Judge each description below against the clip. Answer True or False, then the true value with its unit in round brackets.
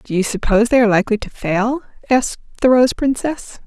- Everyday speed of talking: True (195 wpm)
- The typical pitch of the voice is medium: False (230 Hz)